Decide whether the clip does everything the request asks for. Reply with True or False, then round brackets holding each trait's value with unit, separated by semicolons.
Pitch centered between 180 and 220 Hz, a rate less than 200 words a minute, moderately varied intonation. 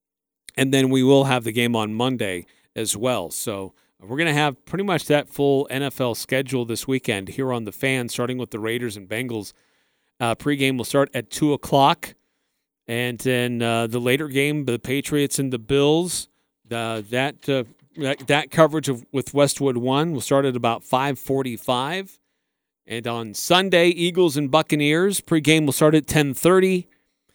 False (135 Hz; 175 wpm; 3.5 semitones)